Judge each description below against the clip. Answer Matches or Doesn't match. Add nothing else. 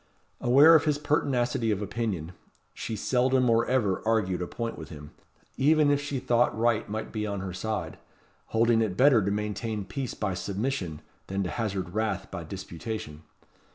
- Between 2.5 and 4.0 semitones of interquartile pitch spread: Doesn't match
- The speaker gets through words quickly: Doesn't match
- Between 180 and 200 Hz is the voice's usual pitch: Doesn't match